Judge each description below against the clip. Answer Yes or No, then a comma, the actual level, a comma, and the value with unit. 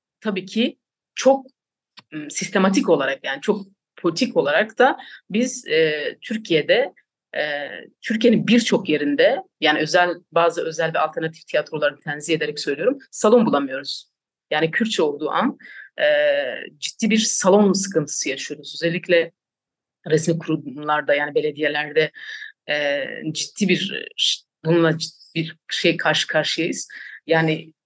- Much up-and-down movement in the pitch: Yes, wide, 6.6 semitones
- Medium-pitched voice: Yes, medium, 170 Hz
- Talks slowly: No, average, 115 wpm